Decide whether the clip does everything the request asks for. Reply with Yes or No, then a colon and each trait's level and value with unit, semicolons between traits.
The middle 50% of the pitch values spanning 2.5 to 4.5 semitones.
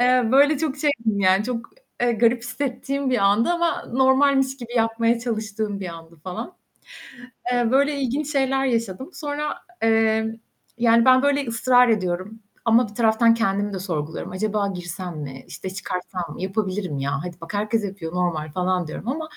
No: wide, 5.4 semitones